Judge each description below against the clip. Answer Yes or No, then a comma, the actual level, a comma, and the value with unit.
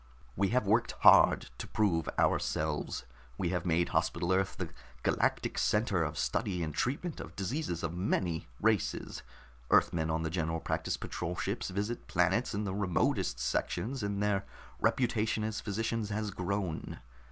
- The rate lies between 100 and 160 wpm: Yes, average, 150 wpm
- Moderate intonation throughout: Yes, average, 4.2 semitones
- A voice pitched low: Yes, very low, 95 Hz